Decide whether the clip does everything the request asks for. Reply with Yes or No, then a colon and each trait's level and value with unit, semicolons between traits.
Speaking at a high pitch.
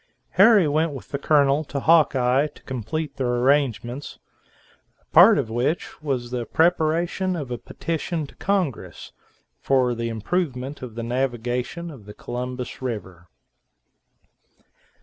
No: low, 135 Hz